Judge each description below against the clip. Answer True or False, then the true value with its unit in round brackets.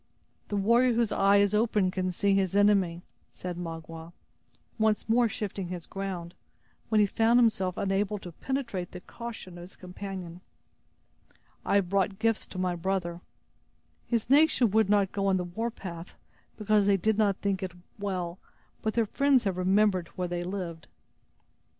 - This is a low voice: False (195 Hz)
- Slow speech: False (160 wpm)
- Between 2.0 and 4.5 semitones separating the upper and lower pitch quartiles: True (3.0 semitones)